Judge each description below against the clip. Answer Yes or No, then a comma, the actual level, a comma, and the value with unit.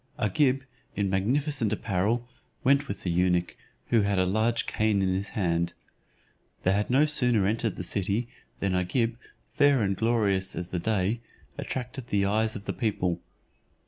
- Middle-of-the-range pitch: No, low, 105 Hz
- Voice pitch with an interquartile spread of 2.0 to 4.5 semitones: Yes, average, 4.0 semitones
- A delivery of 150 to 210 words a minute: Yes, average, 160 wpm